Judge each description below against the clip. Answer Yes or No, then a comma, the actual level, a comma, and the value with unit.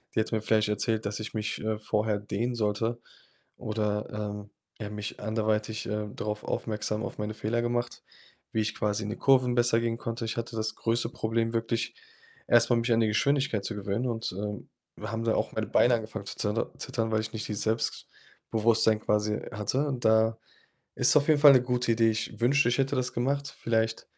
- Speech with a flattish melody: Yes, narrow, 1.9 semitones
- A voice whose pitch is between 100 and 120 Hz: Yes, low, 110 Hz